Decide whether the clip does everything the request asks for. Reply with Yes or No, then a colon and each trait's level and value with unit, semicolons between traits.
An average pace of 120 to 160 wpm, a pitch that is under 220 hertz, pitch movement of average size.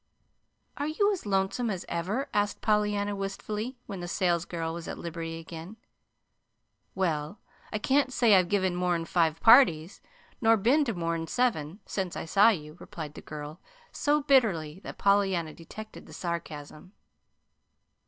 Yes: average, 145 wpm; high, 190 Hz; average, 4.6 semitones